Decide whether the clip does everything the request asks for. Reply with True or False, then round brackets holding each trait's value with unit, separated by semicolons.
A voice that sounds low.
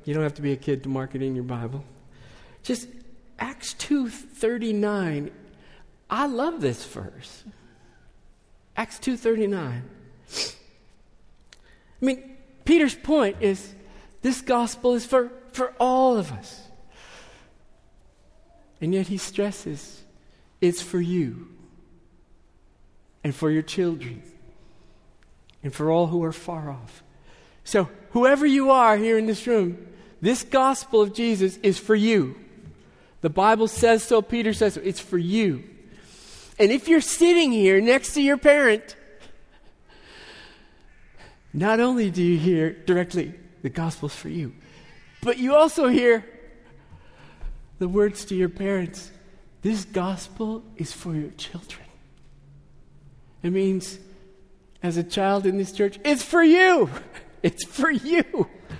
False (200 Hz)